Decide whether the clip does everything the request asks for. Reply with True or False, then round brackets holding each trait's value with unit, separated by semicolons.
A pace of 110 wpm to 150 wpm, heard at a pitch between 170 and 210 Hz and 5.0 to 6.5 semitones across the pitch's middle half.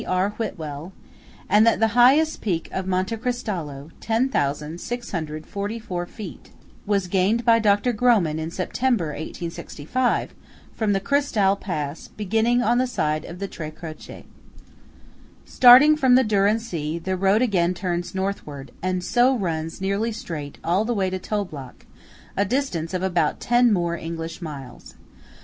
True (140 wpm; 190 Hz; 5.5 semitones)